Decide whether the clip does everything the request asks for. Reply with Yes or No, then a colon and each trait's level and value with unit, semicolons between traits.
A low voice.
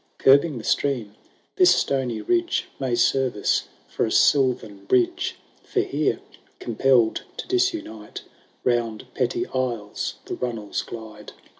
Yes: low, 125 Hz